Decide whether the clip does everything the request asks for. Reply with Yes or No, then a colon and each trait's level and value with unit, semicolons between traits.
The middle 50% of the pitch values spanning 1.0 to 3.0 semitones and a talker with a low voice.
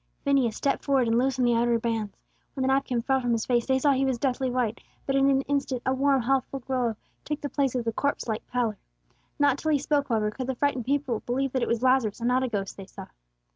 No: narrow, 2.6 semitones; very high, 255 Hz